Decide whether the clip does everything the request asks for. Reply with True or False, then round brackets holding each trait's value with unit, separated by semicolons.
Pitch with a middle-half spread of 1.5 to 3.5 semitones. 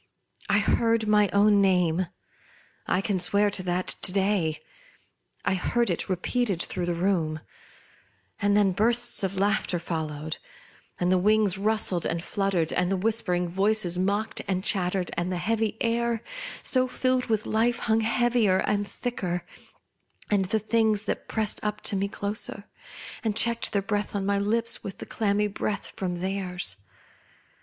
True (3.1 semitones)